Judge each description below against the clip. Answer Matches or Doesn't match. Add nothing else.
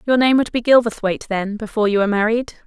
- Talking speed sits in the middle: Doesn't match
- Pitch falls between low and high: Doesn't match